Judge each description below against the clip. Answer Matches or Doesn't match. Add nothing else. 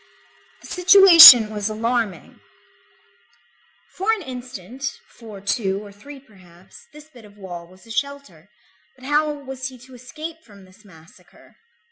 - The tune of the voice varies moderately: Doesn't match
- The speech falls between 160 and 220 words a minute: Doesn't match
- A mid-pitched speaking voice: Doesn't match